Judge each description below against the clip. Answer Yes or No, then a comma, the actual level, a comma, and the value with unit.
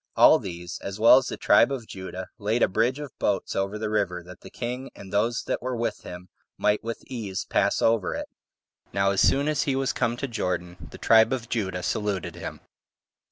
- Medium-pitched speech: No, low, 105 Hz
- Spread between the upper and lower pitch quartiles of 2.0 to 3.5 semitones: No, average, 4.2 semitones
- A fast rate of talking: Yes, fast, 210 wpm